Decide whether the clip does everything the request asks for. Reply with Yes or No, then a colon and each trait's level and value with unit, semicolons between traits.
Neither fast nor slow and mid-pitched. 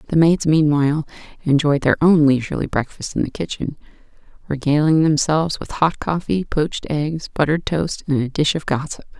Yes: average, 165 wpm; medium, 150 Hz